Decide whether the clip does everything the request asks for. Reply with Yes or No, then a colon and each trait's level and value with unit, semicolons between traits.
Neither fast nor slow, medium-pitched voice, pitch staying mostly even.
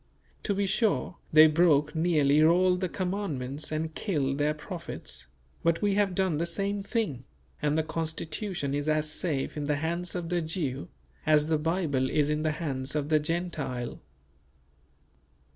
No: average, 160 wpm; medium, 160 Hz; average, 3.2 semitones